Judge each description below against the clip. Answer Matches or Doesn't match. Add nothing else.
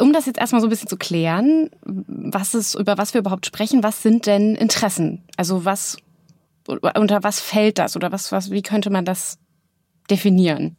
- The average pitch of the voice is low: Doesn't match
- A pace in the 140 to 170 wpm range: Doesn't match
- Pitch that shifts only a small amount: Doesn't match